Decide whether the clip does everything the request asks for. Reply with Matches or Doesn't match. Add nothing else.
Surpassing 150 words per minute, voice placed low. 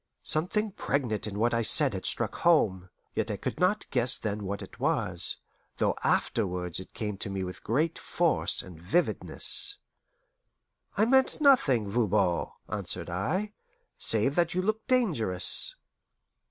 Doesn't match